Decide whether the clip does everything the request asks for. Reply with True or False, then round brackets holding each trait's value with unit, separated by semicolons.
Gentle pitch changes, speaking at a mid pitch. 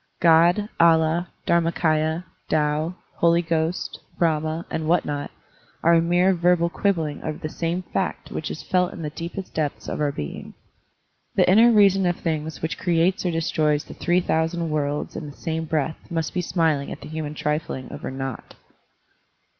True (2.1 semitones; 165 Hz)